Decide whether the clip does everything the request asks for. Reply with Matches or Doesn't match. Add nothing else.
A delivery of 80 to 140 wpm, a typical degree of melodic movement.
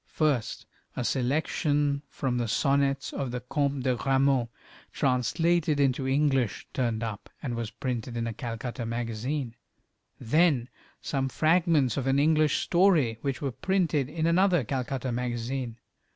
Matches